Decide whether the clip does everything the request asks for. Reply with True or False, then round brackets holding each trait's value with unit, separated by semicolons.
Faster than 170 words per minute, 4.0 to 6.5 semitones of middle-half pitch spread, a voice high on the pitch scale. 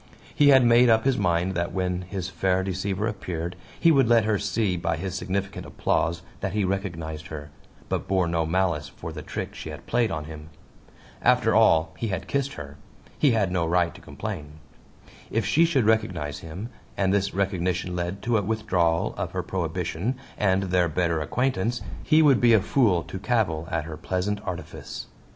False (185 wpm; 4.5 semitones; 95 Hz)